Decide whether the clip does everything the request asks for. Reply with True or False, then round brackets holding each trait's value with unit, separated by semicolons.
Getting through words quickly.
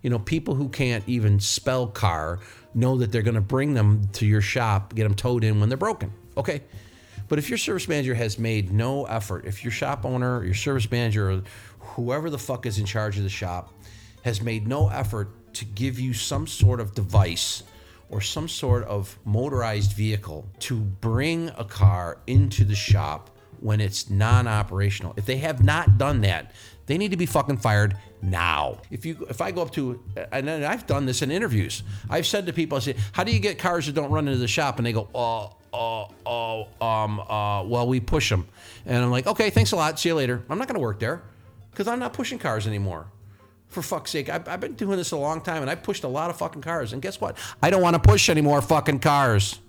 True (230 wpm)